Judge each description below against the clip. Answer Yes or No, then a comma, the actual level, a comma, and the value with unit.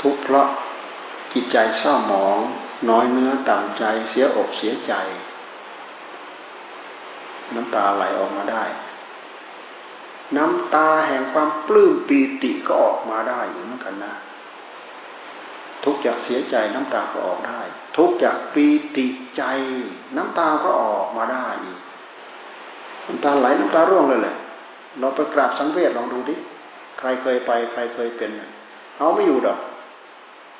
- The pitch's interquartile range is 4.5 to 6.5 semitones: No, average, 3.1 semitones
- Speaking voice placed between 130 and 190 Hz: Yes, medium, 140 Hz